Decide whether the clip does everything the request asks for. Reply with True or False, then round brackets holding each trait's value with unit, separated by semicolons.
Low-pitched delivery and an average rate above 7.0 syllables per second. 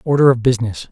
True (125 Hz; 7.4 syllables/s)